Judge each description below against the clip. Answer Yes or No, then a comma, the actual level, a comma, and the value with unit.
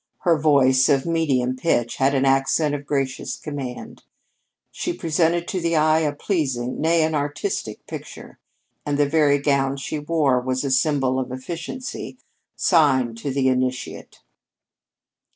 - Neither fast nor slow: Yes, average, 145 wpm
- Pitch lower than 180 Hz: Yes, medium, 140 Hz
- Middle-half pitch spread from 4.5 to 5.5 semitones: No, average, 3.3 semitones